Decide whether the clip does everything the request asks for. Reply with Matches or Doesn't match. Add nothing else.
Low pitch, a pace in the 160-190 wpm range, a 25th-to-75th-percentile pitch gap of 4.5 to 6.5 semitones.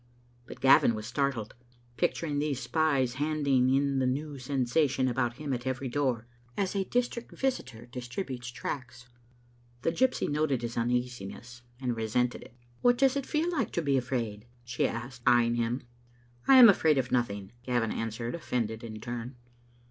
Doesn't match